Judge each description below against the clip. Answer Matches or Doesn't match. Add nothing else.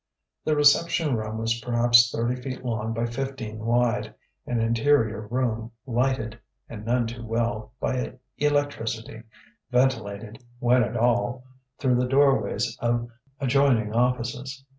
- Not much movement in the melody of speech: Matches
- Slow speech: Matches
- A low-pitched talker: Matches